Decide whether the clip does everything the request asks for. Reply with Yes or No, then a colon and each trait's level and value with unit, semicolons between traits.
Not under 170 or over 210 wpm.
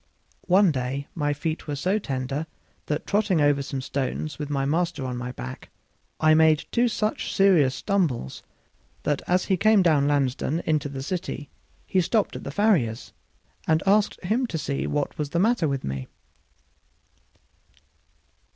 No: average, 160 wpm